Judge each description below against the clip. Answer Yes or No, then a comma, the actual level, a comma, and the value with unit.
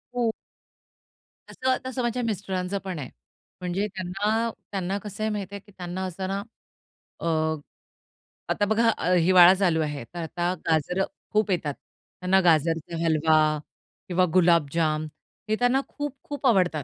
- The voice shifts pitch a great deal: No, average, 3.8 semitones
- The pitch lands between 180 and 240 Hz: Yes, medium, 185 Hz